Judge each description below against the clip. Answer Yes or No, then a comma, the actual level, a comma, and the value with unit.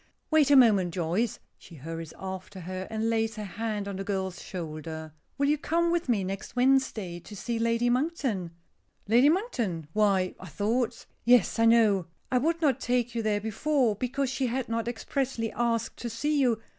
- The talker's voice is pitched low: No, high, 225 Hz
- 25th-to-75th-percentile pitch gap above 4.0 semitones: Yes, average, 4.8 semitones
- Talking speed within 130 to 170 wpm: No, average, 185 wpm